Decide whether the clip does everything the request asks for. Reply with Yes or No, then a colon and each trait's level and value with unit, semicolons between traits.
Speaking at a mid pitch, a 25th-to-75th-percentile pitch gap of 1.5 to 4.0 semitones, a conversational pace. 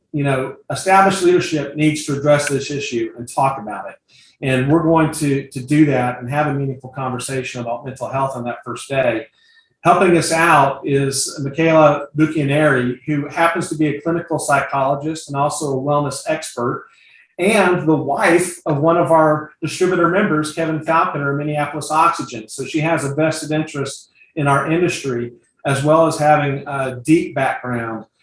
Yes: medium, 150 Hz; average, 2.8 semitones; average, 170 wpm